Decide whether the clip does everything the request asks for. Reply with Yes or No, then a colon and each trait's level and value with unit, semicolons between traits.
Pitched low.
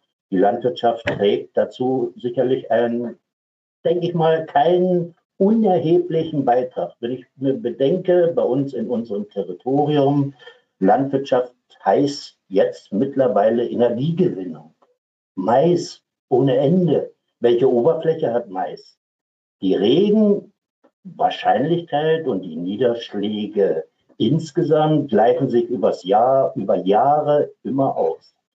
No: medium, 145 Hz